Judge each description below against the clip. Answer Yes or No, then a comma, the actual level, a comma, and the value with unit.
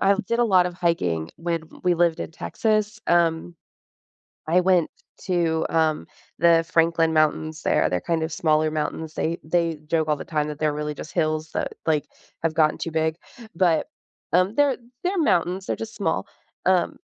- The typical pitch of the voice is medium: Yes, medium, 165 Hz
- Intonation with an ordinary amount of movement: No, narrow, 2.2 semitones